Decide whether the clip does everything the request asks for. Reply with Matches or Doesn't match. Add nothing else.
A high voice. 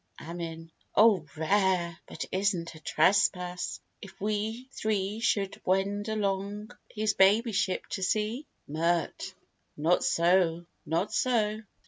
Matches